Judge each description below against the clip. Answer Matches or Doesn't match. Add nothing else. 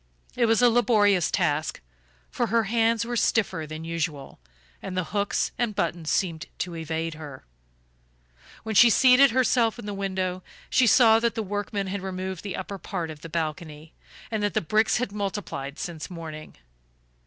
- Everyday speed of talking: Matches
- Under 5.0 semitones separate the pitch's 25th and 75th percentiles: Doesn't match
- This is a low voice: Doesn't match